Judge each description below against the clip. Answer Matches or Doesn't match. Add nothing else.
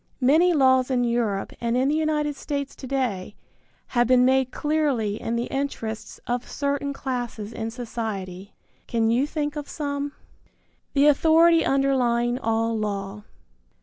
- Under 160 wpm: Matches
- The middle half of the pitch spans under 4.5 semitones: Matches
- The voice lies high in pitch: Matches